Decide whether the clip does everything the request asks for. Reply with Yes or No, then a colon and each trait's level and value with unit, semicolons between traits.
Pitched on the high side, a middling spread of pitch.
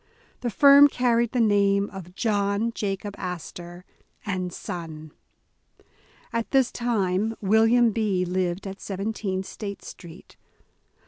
Yes: high, 200 Hz; average, 3.6 semitones